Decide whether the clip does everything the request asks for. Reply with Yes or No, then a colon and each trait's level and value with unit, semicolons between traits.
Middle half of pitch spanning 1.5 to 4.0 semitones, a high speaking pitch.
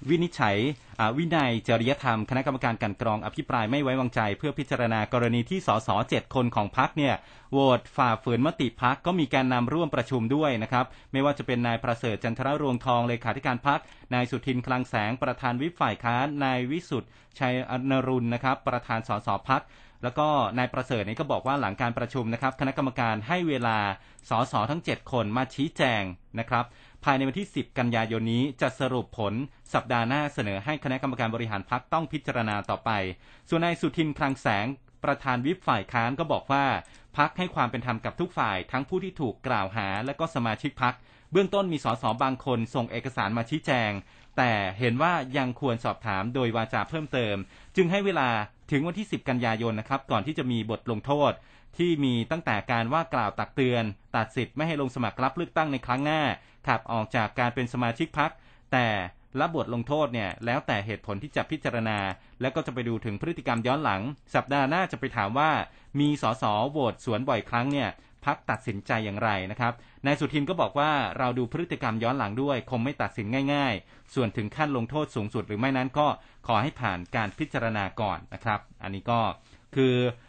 No: average, 3.7 semitones; low, 125 Hz